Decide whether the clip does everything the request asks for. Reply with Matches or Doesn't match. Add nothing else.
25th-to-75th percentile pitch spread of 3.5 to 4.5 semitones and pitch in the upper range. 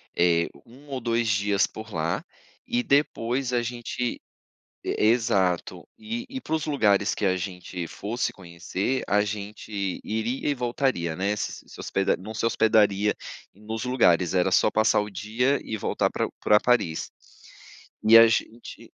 Doesn't match